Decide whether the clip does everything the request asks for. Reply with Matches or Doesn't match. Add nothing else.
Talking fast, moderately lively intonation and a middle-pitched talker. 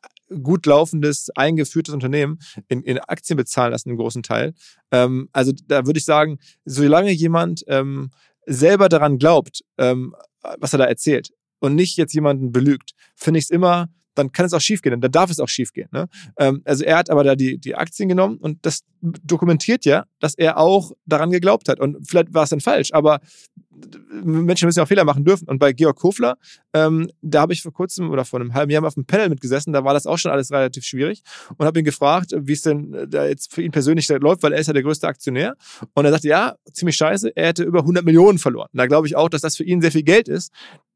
Matches